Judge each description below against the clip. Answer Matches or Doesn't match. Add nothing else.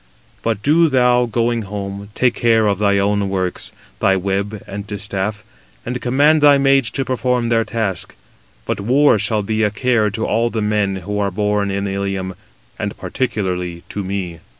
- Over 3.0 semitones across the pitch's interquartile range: Matches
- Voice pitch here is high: Doesn't match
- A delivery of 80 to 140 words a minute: Doesn't match